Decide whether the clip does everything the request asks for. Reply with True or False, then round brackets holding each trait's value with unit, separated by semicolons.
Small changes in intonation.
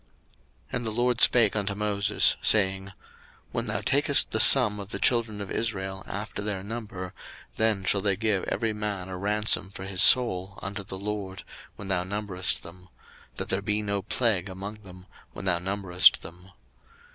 True (2.0 semitones)